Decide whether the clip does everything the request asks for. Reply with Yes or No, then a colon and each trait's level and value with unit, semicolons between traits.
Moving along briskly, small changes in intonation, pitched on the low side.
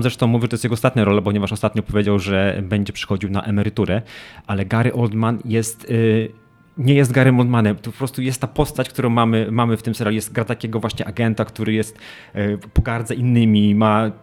Yes: fast, 205 wpm; narrow, 2.2 semitones; low, 115 Hz